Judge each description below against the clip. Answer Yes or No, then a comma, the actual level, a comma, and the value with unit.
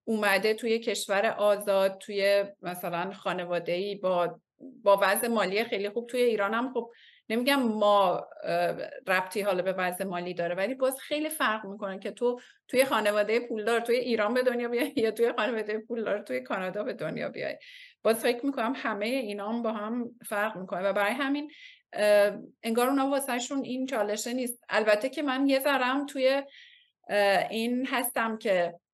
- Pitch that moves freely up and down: No, average, 4.0 semitones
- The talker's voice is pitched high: Yes, high, 225 Hz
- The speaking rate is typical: No, fast, 160 wpm